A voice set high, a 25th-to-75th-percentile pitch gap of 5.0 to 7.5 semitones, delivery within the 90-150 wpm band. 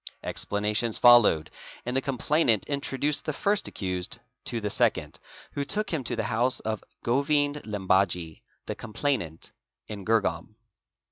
No: low, 115 Hz; wide, 5.5 semitones; average, 140 wpm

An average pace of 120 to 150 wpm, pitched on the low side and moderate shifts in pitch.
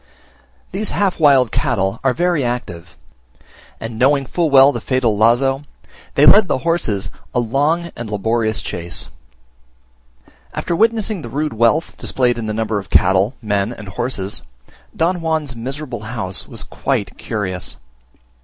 No: average, 145 wpm; low, 120 Hz; wide, 5.8 semitones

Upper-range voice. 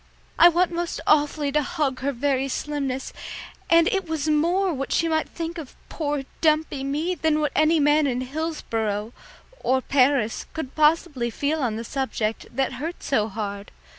Yes: very high, 290 Hz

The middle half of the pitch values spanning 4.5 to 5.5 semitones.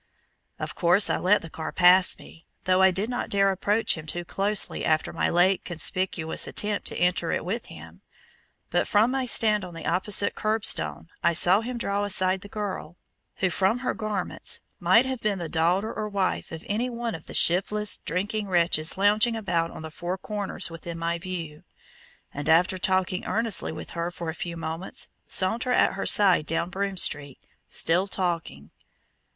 No: average, 3.6 semitones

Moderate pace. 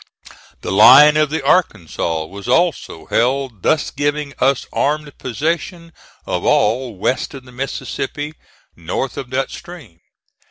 No: slow, 130 wpm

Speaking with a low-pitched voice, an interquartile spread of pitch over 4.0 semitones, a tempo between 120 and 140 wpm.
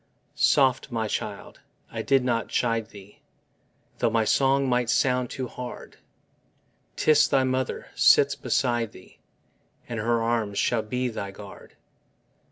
No: low, 120 Hz; narrow, 2.4 semitones; slow, 135 wpm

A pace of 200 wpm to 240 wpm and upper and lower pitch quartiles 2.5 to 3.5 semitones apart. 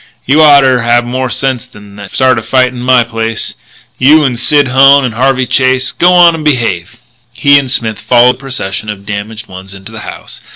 Yes: fast, 205 wpm; average, 3.2 semitones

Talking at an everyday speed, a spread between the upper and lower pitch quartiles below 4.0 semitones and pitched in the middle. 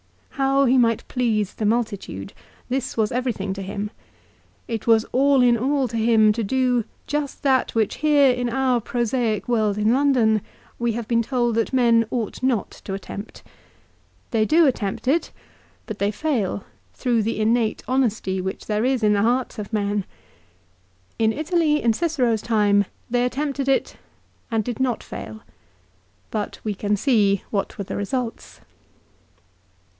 No: average, 160 wpm; average, 3.5 semitones; high, 230 Hz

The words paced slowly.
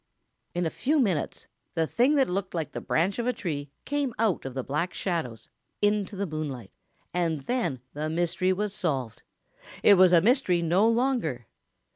No: average, 175 wpm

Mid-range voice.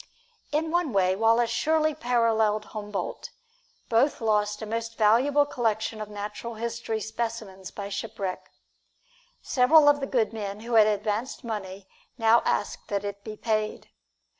No: high, 225 Hz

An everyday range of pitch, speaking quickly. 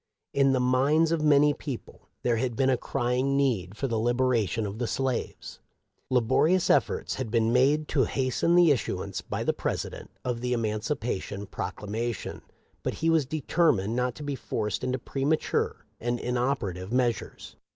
No: average, 3.3 semitones; average, 165 wpm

